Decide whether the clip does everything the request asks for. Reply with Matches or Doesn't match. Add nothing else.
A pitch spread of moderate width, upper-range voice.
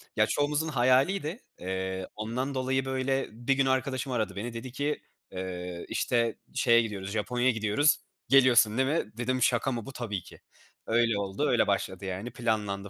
Doesn't match